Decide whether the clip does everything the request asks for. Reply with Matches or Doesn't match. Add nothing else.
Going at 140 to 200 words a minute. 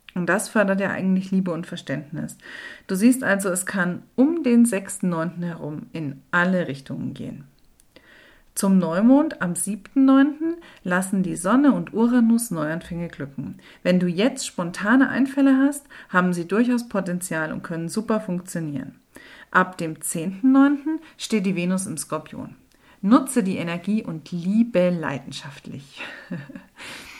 Doesn't match